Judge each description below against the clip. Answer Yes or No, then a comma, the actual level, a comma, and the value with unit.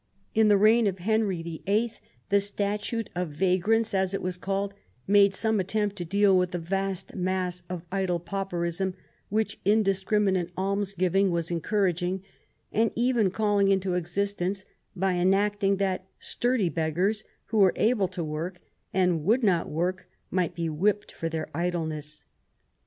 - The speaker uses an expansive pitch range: No, narrow, 2.5 semitones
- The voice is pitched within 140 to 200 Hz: Yes, high, 190 Hz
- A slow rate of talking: No, average, 155 wpm